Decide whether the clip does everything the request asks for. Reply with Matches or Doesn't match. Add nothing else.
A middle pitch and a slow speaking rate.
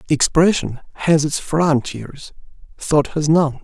Matches